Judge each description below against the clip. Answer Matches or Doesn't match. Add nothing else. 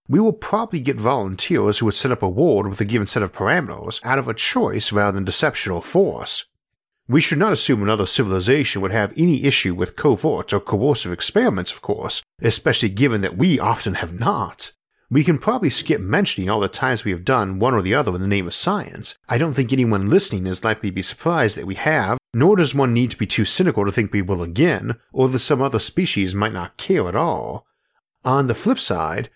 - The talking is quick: Matches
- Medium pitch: Doesn't match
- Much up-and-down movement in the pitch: Matches